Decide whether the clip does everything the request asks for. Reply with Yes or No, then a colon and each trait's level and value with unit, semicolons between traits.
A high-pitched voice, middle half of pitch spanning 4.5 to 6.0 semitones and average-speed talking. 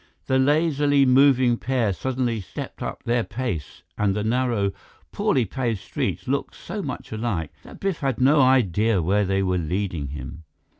No: low, 115 Hz; average, 5.3 semitones; average, 160 wpm